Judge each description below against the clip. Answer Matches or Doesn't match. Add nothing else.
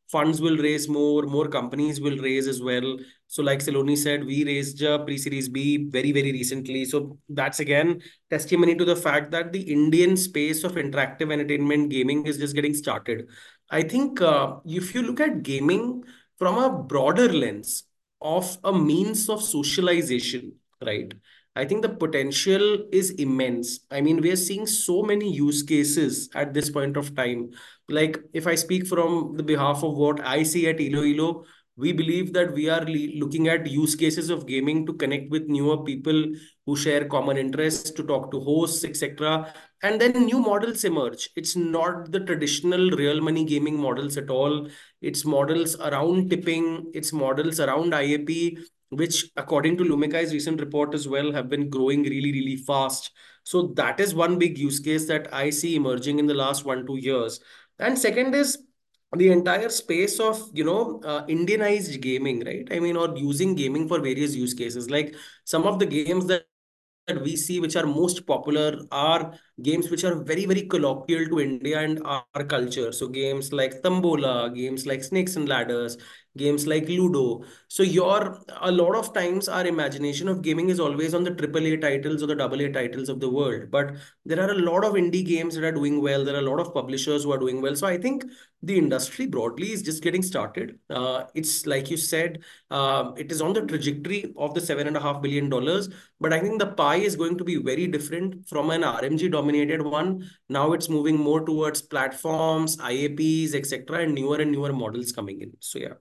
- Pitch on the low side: Doesn't match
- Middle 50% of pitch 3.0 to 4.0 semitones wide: Matches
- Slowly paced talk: Doesn't match